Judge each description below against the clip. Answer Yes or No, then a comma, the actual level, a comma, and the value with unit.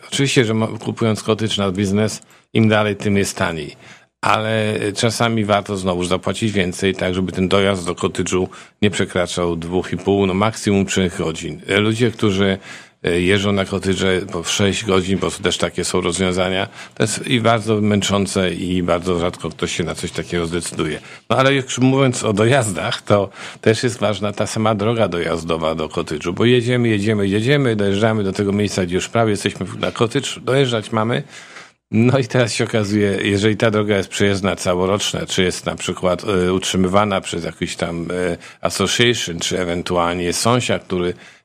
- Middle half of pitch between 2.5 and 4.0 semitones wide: Yes, average, 3.3 semitones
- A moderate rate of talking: No, fast, 165 wpm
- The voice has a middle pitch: No, low, 100 Hz